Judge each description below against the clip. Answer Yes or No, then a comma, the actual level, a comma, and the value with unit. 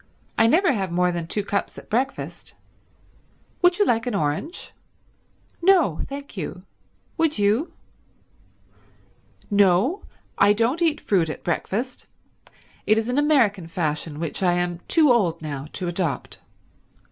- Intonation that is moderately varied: No, wide, 8.0 semitones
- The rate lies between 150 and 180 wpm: No, slow, 135 wpm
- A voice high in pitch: Yes, high, 205 Hz